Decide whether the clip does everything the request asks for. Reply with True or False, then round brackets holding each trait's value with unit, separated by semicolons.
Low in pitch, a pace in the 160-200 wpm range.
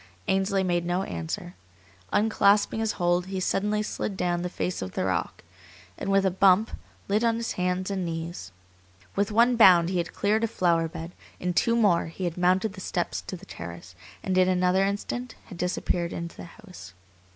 False (185 Hz; 190 wpm)